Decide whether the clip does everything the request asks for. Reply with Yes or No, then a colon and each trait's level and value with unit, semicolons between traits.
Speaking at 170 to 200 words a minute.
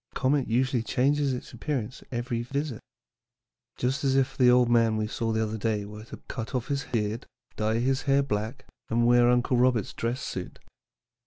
Yes: average, 190 wpm